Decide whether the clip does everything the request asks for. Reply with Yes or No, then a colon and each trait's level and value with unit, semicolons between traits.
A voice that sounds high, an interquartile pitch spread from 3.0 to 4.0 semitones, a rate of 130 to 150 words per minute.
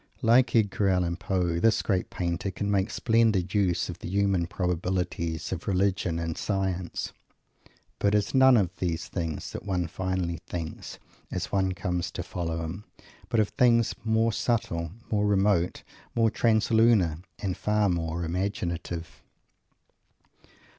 No: very low, 95 Hz; average, 3.3 semitones; average, 140 wpm